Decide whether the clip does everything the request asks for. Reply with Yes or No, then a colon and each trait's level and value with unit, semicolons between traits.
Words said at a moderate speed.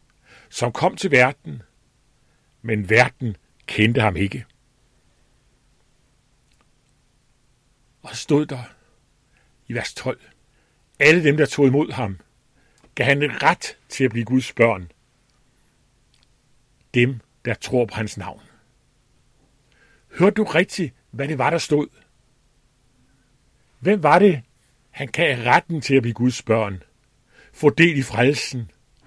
No: slow, 120 wpm